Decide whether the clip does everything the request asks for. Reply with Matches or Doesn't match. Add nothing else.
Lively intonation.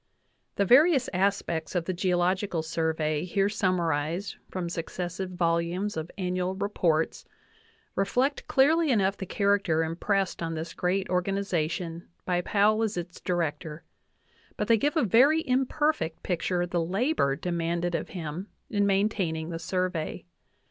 Doesn't match